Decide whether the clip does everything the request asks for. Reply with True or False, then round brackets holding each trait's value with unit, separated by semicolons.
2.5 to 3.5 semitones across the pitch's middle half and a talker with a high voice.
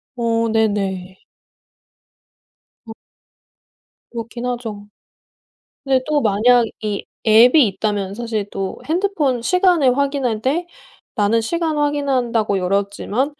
False (5.1 semitones; 235 Hz)